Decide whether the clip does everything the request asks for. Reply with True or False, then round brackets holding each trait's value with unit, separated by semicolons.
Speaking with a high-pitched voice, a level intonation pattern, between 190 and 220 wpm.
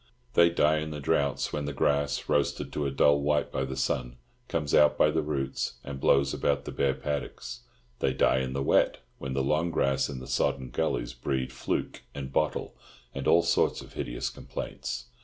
False (70 Hz; 2.1 semitones; 195 wpm)